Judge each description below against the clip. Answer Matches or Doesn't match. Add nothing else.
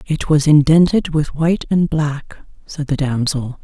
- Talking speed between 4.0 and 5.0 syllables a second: Matches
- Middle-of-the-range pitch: Matches